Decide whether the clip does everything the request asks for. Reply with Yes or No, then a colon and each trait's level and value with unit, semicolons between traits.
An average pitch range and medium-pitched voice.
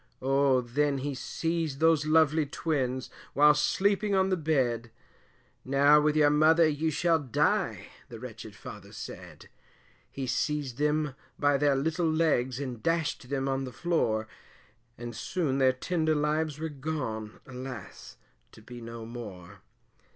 Yes: average, 4.0 semitones; medium, 145 Hz